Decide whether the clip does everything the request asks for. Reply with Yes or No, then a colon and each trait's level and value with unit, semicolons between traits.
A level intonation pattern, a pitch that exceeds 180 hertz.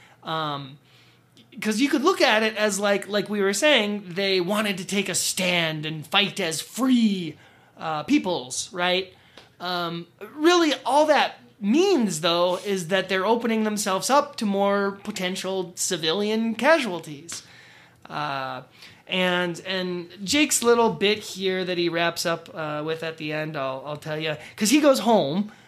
No: average, 4.2 semitones; high, 190 Hz